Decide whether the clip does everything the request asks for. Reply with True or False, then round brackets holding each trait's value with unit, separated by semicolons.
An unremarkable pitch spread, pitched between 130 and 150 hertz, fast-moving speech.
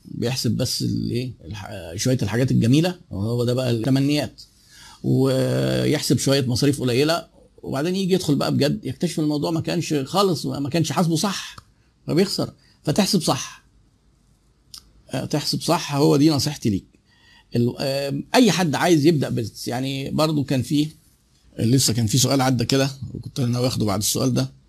True (4.1 semitones; 135 Hz; 140 wpm)